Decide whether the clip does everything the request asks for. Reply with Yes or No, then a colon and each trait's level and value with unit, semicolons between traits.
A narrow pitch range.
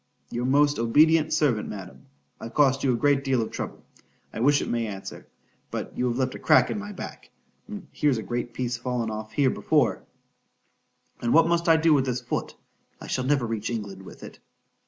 No: average, 4.1 semitones